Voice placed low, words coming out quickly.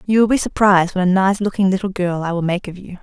No: high, 190 Hz; fast, 295 wpm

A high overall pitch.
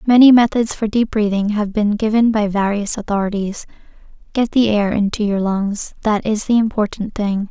Yes: high, 210 Hz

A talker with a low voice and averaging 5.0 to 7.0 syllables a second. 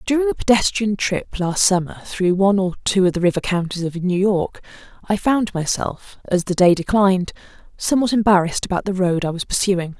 No: high, 190 Hz; 5.6 syllables/s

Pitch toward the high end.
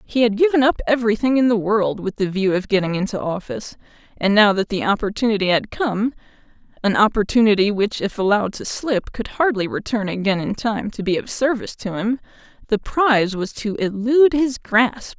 Yes: high, 215 Hz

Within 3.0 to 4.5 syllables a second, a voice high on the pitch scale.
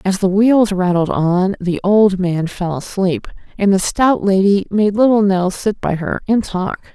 Yes: 4.1 syllables/s; high, 195 Hz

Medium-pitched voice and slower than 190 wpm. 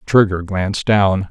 No: low, 100 Hz; average, 140 wpm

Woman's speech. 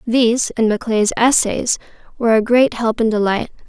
Yes: female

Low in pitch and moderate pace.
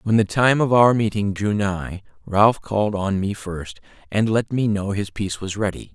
No: low, 105 Hz; fast, 210 wpm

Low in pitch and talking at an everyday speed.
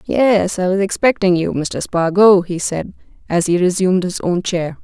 No: medium, 185 Hz; average, 185 wpm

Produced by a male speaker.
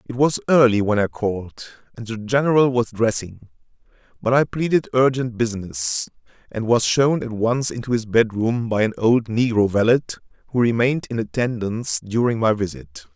Yes: male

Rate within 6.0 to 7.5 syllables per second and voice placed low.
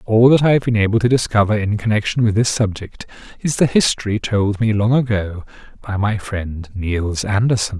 No: 5.2 syllables/s; low, 105 Hz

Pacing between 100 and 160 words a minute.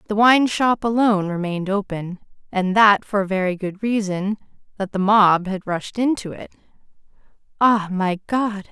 Yes: average, 150 wpm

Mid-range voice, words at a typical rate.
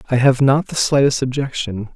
No: low, 130 Hz; average, 185 wpm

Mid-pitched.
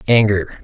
No: low, 100 Hz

